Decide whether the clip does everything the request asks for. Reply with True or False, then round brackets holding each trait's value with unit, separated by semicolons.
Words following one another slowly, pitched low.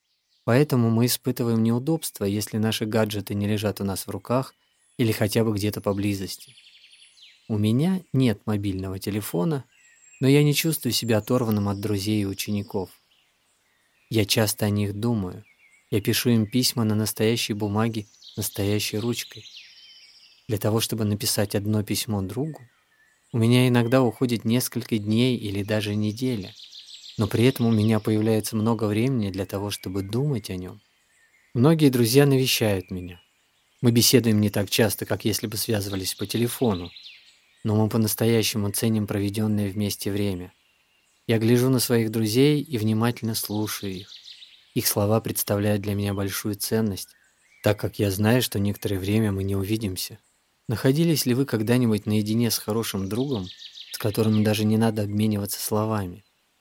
False (150 wpm; 110 Hz)